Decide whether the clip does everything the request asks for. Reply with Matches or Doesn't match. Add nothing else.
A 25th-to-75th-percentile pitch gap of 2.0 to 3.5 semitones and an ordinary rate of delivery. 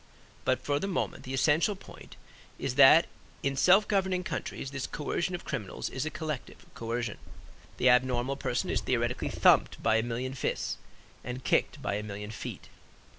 Doesn't match